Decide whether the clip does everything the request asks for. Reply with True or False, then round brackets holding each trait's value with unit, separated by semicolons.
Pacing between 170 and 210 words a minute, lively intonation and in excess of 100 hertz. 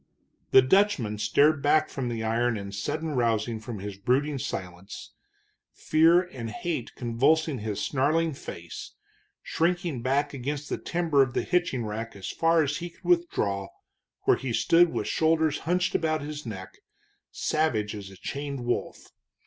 False (155 wpm; 6.1 semitones; 135 Hz)